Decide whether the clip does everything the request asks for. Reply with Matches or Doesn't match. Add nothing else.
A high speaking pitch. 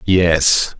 Doesn't match